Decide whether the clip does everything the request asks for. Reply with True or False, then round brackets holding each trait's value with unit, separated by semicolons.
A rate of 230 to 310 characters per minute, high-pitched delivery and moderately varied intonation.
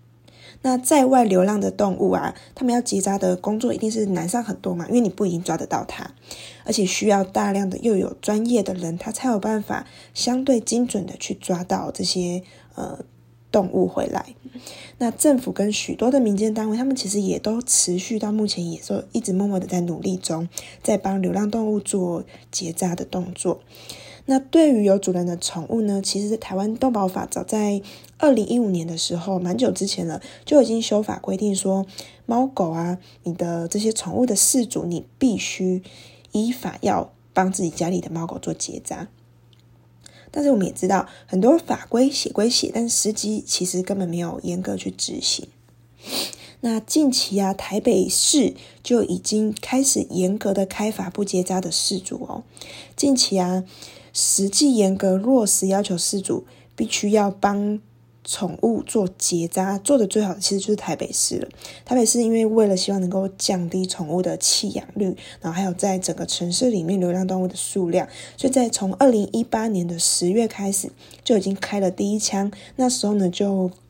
True (270 characters per minute; 195 Hz; 3.6 semitones)